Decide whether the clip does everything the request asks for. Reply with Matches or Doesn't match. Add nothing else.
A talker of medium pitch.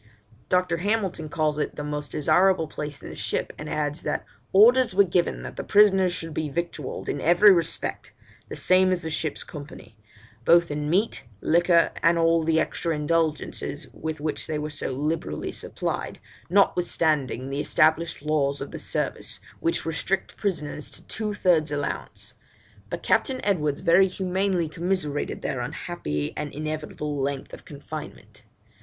Matches